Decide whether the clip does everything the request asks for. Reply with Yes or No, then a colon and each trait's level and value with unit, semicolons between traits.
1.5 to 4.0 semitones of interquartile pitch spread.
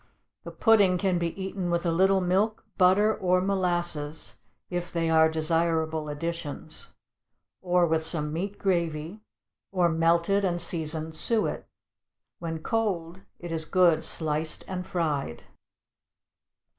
Yes: narrow, 2.6 semitones